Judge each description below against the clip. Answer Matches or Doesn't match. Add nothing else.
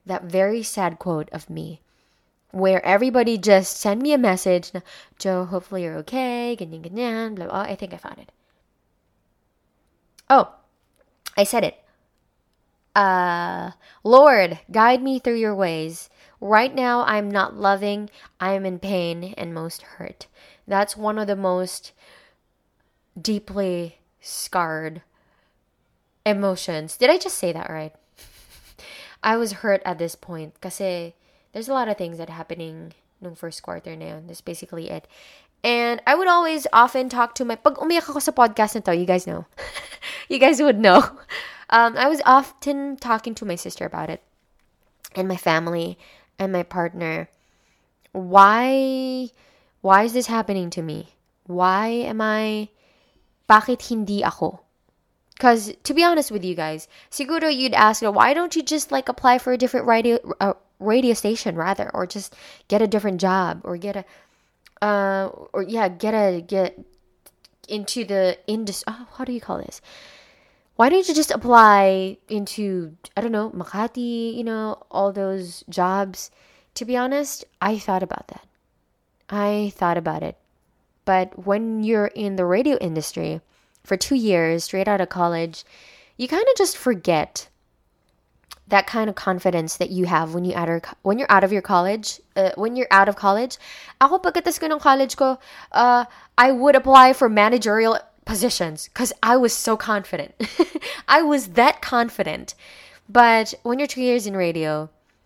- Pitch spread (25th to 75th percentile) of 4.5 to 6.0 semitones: Matches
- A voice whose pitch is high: Matches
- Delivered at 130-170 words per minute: Matches